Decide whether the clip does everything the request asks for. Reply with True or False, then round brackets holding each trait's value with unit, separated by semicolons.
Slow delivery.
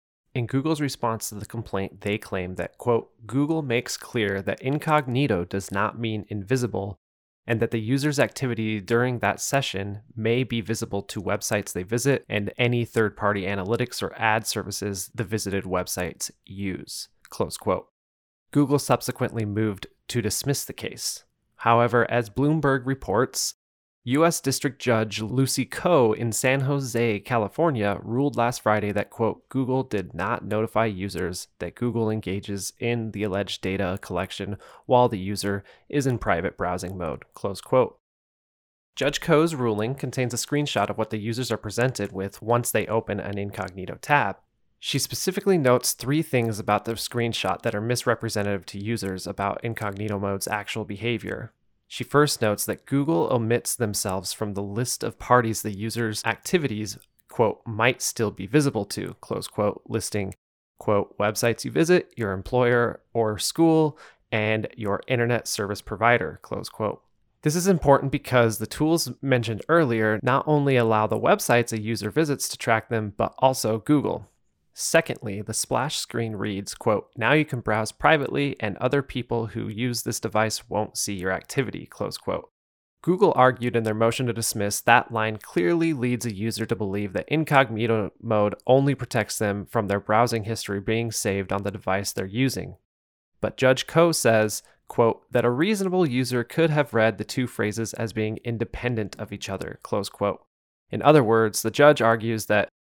False (165 wpm)